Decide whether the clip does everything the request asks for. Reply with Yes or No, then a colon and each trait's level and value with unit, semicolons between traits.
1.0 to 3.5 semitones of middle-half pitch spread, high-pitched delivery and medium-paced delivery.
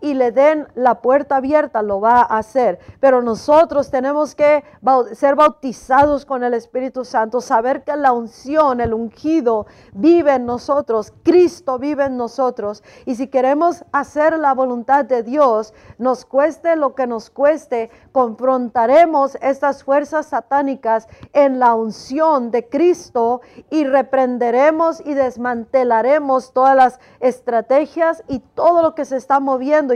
Yes: average, 3.1 semitones; very high, 265 Hz; average, 140 wpm